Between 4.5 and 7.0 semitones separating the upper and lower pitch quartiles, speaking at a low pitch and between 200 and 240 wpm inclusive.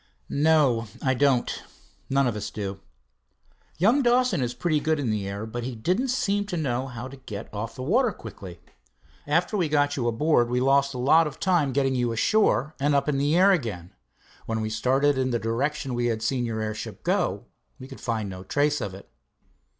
Yes: average, 5.0 semitones; low, 130 Hz; fast, 205 wpm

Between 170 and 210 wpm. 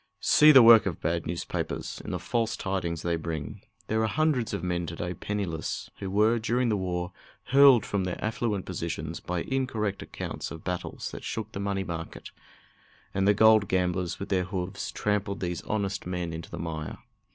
Yes: average, 185 wpm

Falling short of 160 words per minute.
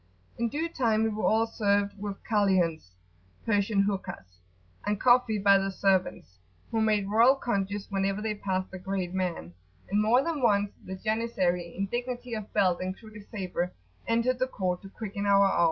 No: average, 175 wpm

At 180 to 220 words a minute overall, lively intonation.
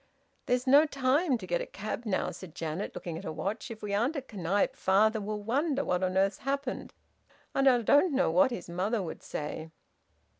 Yes: average, 200 wpm; wide, 6.0 semitones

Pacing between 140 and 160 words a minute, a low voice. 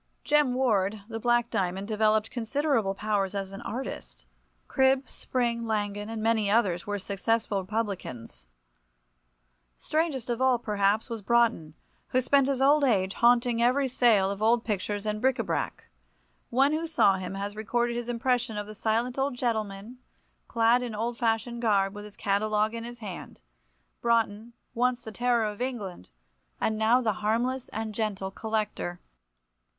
No: average, 155 wpm; high, 225 Hz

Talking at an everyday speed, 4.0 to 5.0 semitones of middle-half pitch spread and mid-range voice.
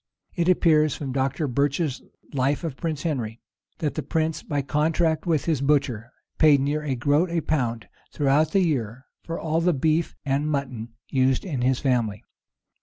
No: average, 170 wpm; average, 3.3 semitones; medium, 145 Hz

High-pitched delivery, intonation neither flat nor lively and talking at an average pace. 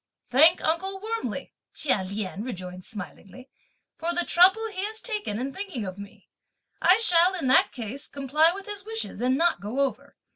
No: very high, 315 Hz; wide, 8.5 semitones; average, 175 wpm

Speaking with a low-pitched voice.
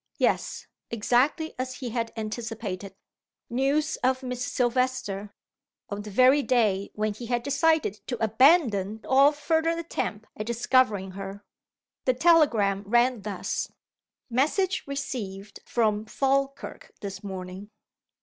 No: high, 240 Hz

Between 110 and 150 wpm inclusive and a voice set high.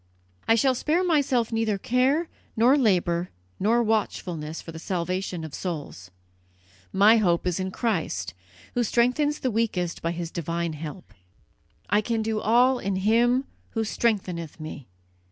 Yes: average, 145 wpm; high, 210 Hz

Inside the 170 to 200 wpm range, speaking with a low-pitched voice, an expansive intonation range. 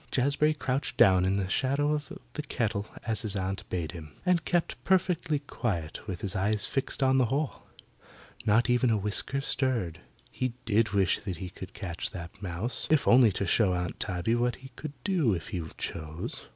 Yes: average, 185 wpm; low, 110 Hz; wide, 6.3 semitones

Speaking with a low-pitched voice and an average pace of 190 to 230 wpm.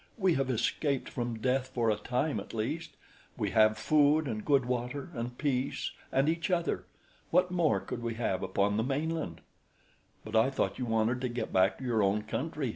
Yes: low, 125 Hz; average, 195 wpm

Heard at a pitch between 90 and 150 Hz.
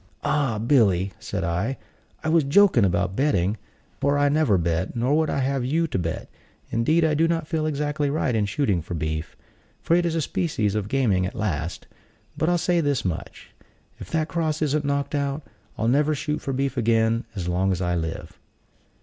Yes: low, 135 Hz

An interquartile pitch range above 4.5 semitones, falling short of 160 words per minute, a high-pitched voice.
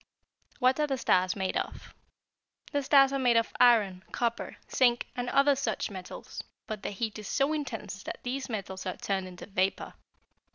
No: wide, 5.4 semitones; average, 175 wpm; high, 230 Hz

